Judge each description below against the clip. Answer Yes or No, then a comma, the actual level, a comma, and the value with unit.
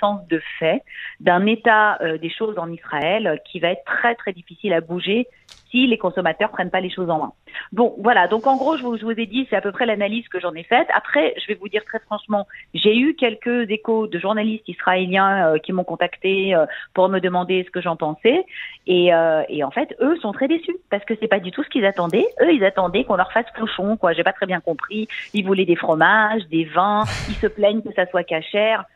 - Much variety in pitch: No, average, 3.7 semitones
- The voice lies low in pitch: No, high, 200 Hz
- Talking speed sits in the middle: No, fast, 240 wpm